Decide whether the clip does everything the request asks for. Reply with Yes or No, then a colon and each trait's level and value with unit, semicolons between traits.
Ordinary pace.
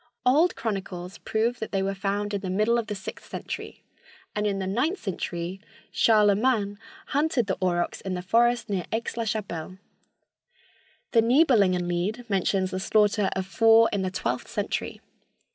Yes: average, 160 wpm